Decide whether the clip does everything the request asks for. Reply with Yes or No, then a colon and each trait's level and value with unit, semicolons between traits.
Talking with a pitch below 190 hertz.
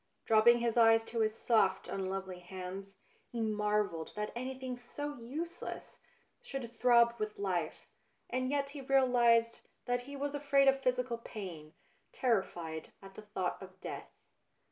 No: high, 230 Hz